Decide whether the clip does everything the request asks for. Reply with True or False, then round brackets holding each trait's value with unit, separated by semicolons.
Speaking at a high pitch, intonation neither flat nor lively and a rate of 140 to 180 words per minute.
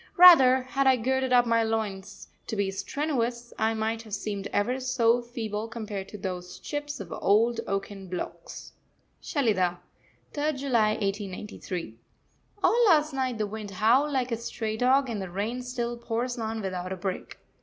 True (225 Hz; 4.0 semitones; 165 wpm)